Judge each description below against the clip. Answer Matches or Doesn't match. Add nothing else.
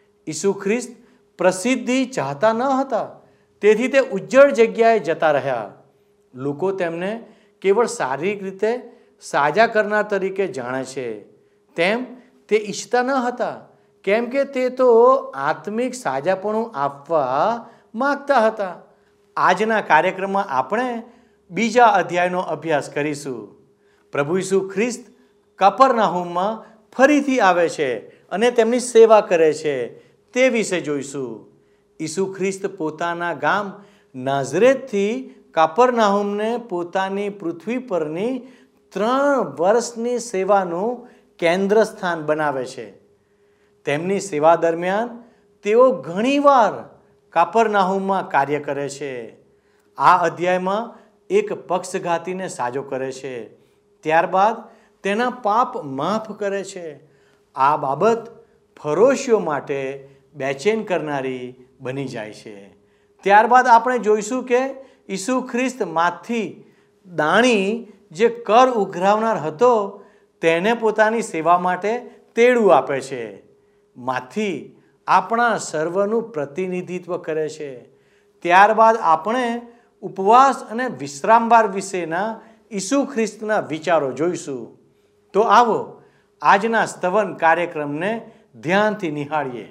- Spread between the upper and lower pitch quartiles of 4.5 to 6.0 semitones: Matches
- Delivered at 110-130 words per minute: Doesn't match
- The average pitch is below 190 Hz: Doesn't match